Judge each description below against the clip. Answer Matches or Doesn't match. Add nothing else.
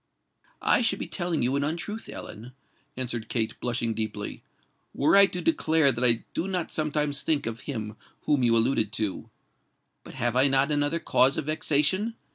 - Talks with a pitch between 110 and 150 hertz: Matches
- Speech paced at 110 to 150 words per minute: Doesn't match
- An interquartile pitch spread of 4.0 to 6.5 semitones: Matches